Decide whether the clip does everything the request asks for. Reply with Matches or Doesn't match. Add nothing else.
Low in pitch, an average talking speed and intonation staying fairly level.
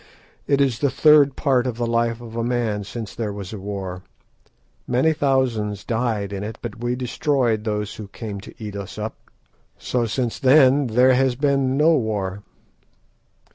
Doesn't match